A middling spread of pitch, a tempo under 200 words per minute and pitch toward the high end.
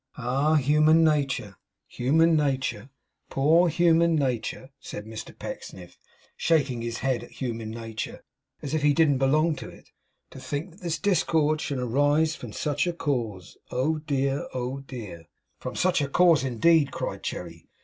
No: average, 4.4 semitones; average, 155 wpm; medium, 140 Hz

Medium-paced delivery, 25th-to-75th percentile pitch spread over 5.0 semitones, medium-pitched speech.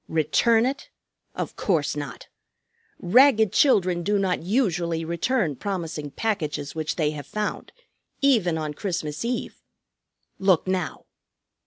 No: slow, 120 wpm; wide, 5.4 semitones; medium, 180 Hz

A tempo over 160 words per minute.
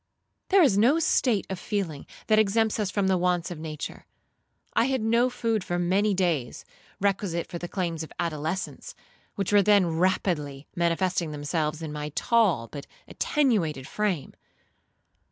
No: average, 155 wpm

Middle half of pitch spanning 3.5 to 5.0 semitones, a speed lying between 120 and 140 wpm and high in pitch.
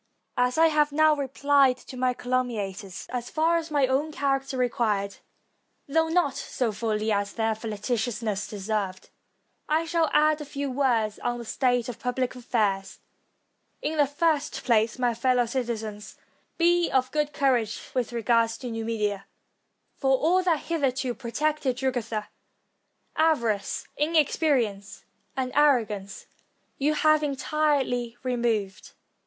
Yes: average, 4.7 semitones; slow, 135 wpm; very high, 255 Hz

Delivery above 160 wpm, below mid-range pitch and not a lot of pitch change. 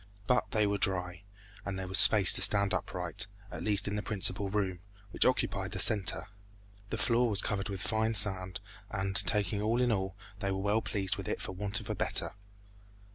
Yes: average, 200 wpm; low, 100 Hz; narrow, 1.9 semitones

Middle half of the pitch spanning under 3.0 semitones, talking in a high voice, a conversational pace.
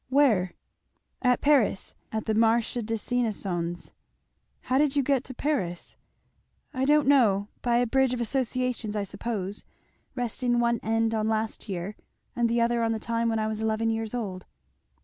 Yes: narrow, 2.6 semitones; high, 230 Hz; average, 170 wpm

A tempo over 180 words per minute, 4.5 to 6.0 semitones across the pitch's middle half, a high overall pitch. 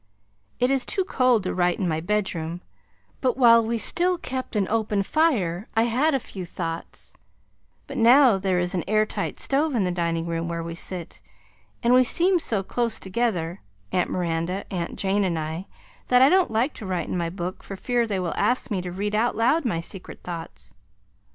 Yes: average, 200 wpm; wide, 5.6 semitones; high, 200 Hz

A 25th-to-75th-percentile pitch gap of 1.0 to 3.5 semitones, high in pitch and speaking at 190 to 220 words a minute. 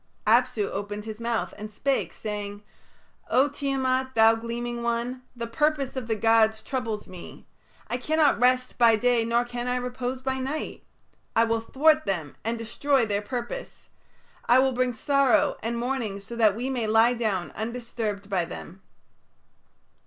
No: average, 2.8 semitones; high, 235 Hz; average, 160 wpm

